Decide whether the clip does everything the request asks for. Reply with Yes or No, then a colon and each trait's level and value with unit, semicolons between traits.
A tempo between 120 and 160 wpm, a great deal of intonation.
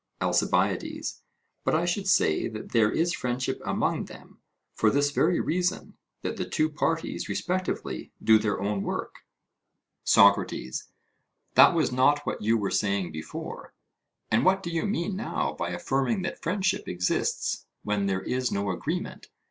Yes: average, 150 wpm; wide, 9.0 semitones